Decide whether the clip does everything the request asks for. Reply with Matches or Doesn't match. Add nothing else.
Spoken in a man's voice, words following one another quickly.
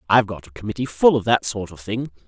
Matches